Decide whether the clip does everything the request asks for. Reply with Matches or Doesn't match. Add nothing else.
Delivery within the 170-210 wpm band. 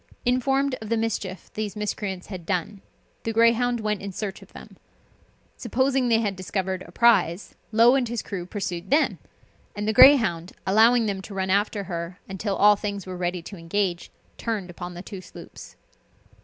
Matches